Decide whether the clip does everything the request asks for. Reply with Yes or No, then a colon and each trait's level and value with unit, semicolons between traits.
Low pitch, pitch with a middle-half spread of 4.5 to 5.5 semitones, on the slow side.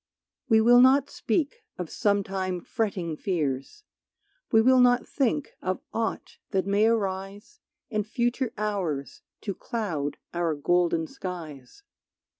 No: high, 200 Hz; average, 5.1 semitones; slow, 120 wpm